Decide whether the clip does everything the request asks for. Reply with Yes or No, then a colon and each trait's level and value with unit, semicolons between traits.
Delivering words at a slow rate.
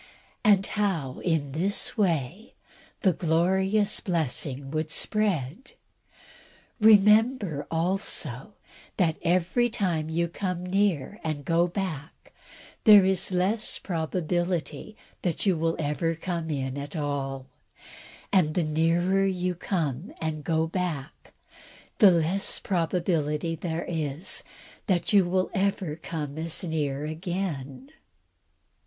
Yes: slow, 110 wpm